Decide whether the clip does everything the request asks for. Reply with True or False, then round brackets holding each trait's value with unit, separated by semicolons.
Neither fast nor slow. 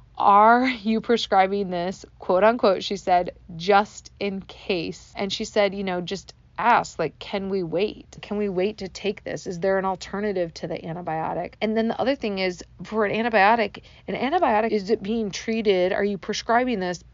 True (190 wpm)